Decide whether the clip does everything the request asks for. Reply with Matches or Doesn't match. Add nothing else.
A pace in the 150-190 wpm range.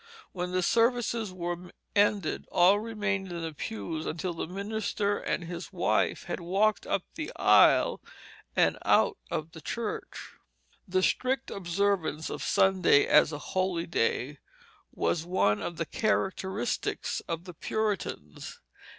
Doesn't match